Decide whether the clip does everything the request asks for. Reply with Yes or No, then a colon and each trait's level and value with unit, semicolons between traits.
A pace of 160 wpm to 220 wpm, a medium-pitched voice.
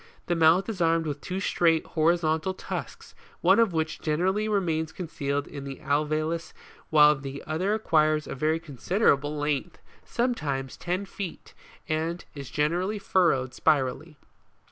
No: average, 145 wpm; medium, 160 Hz